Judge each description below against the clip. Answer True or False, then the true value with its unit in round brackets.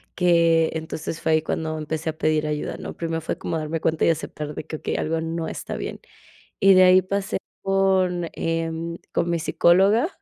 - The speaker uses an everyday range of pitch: False (2.1 semitones)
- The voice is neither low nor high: True (165 Hz)